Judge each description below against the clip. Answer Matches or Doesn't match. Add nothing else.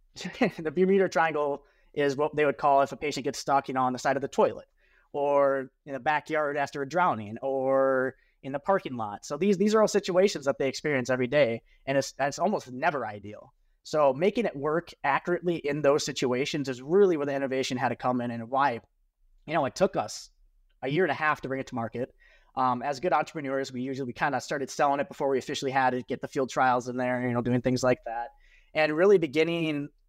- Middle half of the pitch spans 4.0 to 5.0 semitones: Doesn't match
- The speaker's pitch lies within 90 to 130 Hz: Doesn't match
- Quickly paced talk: Matches